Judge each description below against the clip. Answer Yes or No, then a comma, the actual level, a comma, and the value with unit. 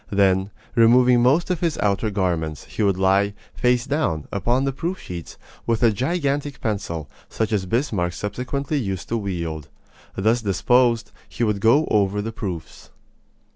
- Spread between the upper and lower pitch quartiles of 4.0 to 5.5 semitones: Yes, average, 4.6 semitones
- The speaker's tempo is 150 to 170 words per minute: Yes, average, 155 wpm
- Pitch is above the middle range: No, low, 110 Hz